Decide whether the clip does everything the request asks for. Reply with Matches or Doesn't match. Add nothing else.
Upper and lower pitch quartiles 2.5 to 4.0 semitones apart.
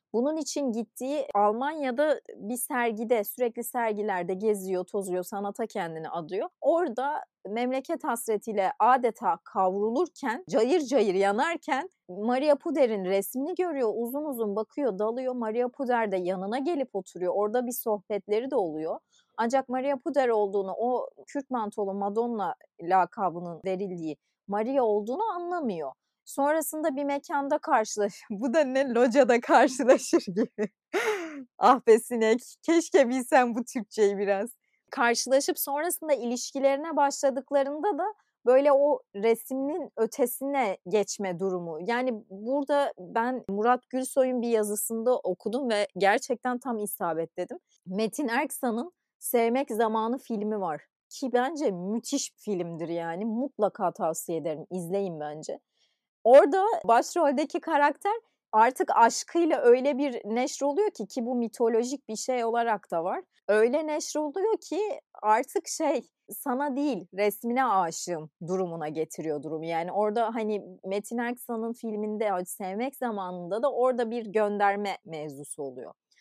Doesn't match